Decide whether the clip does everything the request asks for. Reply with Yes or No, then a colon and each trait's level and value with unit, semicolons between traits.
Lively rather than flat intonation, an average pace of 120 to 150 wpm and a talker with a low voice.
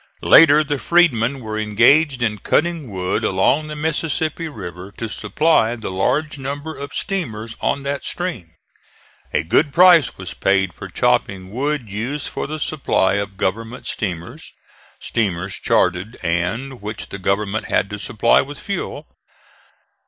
Yes: wide, 7.1 semitones; average, 145 wpm; low, 115 Hz